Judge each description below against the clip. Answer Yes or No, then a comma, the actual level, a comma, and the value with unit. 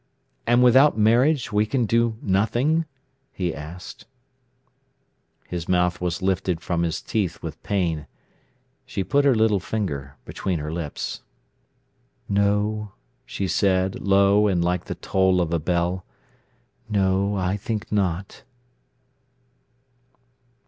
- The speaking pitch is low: Yes, very low, 95 Hz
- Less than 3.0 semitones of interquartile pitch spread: No, average, 3.3 semitones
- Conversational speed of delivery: No, slow, 120 wpm